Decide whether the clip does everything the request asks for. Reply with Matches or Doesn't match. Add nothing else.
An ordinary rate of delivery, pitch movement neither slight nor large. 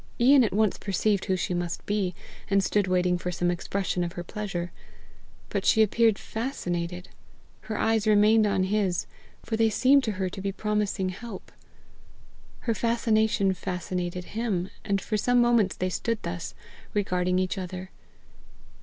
Matches